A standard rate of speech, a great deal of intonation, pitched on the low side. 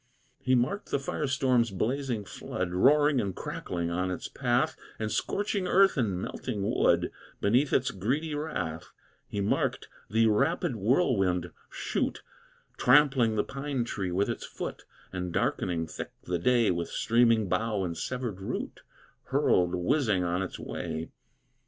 Yes: average, 145 wpm; wide, 6.5 semitones; low, 110 Hz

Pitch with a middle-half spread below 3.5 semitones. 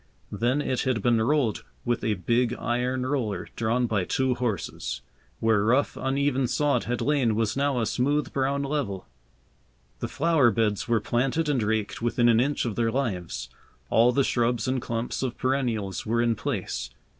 Yes: average, 3.1 semitones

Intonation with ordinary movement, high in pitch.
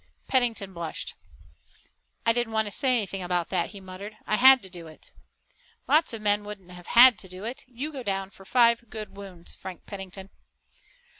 Yes: average, 3.8 semitones; high, 205 Hz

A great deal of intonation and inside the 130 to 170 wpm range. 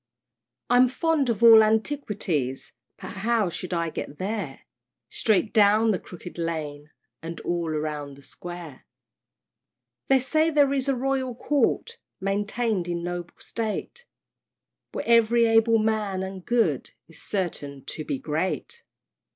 Yes: wide, 5.9 semitones; slow, 135 wpm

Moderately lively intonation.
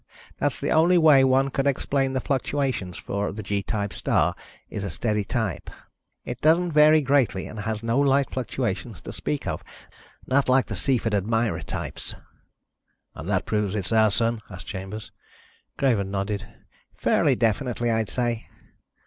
Yes: average, 4.7 semitones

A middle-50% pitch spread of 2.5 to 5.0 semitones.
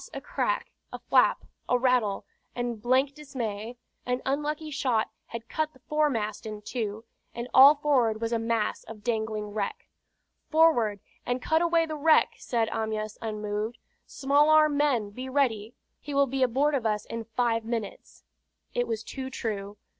Yes: average, 4.5 semitones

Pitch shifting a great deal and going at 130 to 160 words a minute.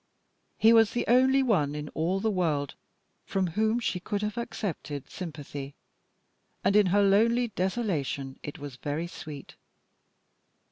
Yes: wide, 6.8 semitones; average, 140 wpm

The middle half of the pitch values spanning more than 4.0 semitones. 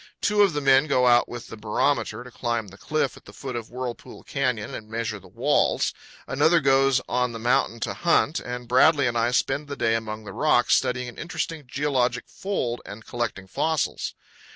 No: average, 3.3 semitones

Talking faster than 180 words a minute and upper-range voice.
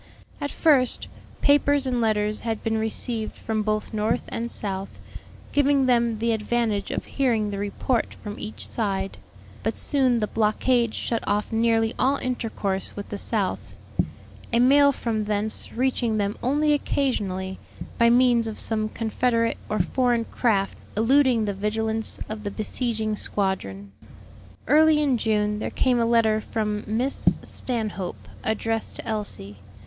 No: average, 145 wpm; high, 225 Hz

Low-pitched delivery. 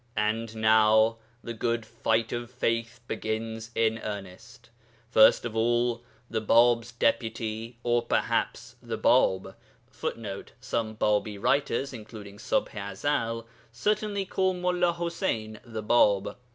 Yes: low, 115 Hz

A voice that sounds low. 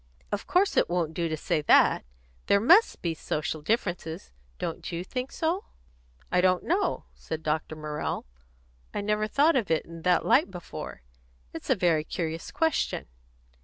No: medium, 180 Hz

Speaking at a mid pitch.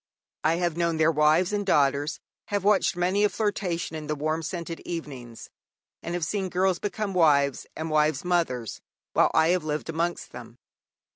Yes: medium, 165 Hz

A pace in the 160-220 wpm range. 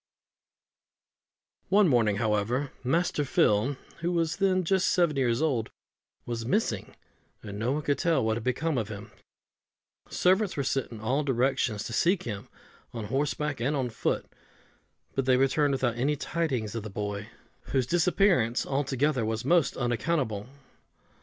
No: average, 150 wpm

